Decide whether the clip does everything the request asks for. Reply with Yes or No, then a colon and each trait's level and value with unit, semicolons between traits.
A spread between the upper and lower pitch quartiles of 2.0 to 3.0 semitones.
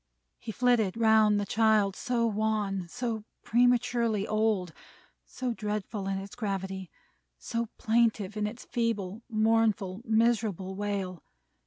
Yes: average, 2.7 semitones